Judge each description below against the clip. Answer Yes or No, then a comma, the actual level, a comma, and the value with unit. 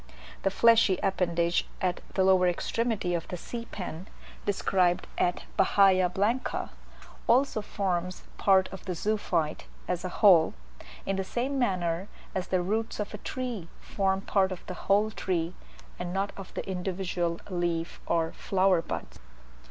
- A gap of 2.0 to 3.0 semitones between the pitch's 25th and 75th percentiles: Yes, narrow, 2.4 semitones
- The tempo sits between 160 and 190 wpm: No, average, 150 wpm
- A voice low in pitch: No, high, 190 Hz